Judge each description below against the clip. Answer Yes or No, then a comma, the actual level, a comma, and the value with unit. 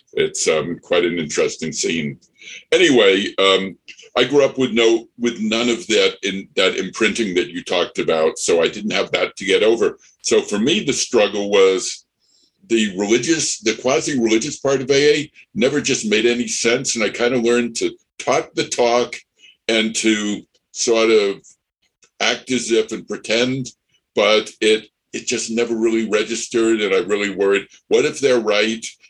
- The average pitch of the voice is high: No, low, 120 Hz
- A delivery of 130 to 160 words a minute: No, average, 170 wpm